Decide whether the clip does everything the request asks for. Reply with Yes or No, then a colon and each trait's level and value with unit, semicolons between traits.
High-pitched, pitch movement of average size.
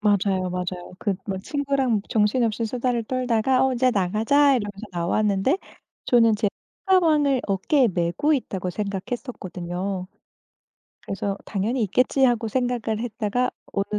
Yes: high, 220 Hz; average, 4.4 semitones